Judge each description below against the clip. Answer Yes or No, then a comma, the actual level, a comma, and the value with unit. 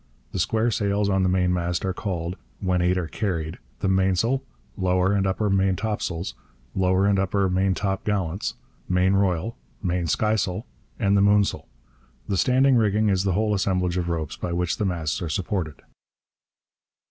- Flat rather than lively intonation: Yes, narrow, 2.1 semitones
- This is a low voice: Yes, very low, 95 Hz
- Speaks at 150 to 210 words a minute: Yes, average, 155 wpm